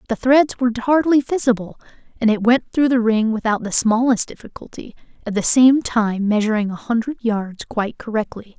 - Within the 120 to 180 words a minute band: Yes, average, 175 wpm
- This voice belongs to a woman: Yes, female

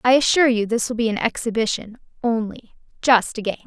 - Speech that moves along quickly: No, average, 195 wpm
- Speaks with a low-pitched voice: No, high, 230 Hz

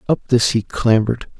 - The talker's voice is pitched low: Yes, low, 115 Hz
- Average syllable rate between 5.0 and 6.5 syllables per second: Yes, 5.7 syllables/s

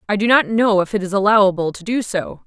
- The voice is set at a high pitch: Yes, high, 205 Hz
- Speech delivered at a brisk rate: Yes, fast, 270 wpm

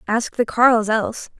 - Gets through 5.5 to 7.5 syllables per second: No, 5.1 syllables/s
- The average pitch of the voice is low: No, high, 230 Hz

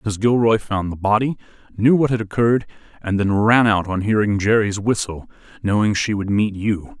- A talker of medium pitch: No, low, 105 Hz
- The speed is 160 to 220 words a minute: Yes, average, 190 wpm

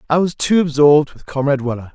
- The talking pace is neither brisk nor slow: No, fast, 215 wpm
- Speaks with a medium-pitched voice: Yes, medium, 145 Hz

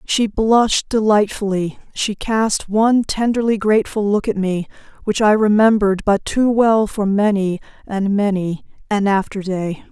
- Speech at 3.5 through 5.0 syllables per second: Yes, 4.5 syllables/s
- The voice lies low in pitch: No, high, 205 Hz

